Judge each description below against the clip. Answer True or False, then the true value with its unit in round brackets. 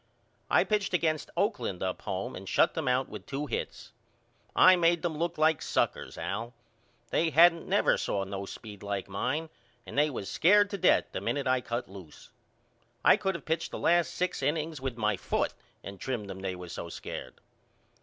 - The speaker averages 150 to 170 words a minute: False (190 wpm)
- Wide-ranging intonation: True (8.9 semitones)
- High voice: False (135 Hz)